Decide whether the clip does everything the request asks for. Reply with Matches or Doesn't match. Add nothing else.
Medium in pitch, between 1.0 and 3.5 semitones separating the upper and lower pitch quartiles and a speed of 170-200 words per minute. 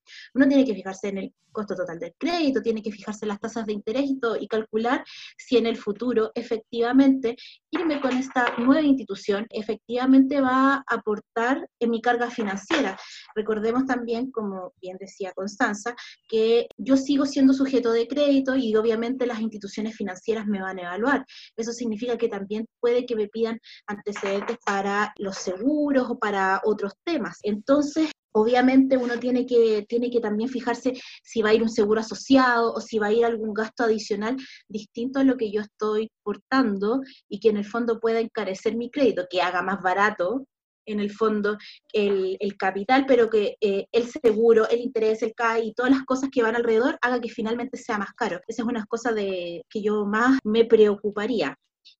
Doesn't match